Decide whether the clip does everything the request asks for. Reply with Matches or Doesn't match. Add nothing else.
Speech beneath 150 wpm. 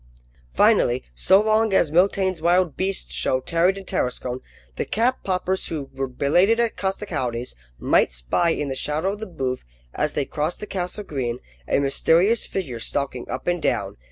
Doesn't match